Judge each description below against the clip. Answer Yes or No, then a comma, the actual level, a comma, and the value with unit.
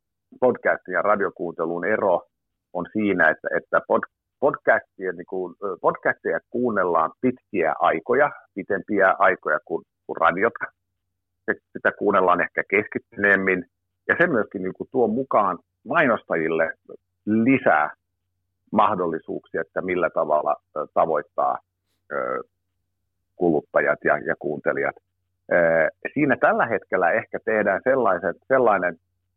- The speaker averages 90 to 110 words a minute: Yes, average, 100 wpm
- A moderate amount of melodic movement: No, narrow, 0.7 semitones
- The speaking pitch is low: Yes, very low, 95 Hz